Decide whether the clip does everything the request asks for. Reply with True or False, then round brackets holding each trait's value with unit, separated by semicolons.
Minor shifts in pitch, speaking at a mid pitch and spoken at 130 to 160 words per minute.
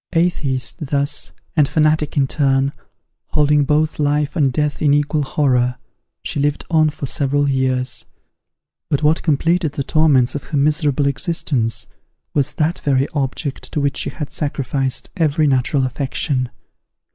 True (2.1 semitones; 145 Hz; 145 wpm)